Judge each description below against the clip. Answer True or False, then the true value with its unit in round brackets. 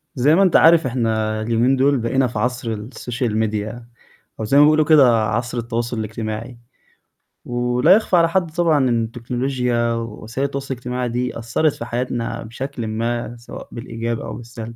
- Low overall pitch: True (120 Hz)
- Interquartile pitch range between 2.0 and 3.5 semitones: True (2.5 semitones)